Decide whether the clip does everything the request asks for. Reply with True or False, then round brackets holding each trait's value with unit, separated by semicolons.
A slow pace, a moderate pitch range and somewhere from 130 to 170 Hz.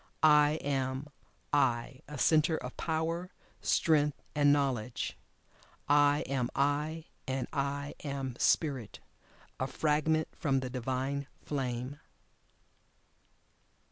False (100 wpm; 2.2 semitones; 140 Hz)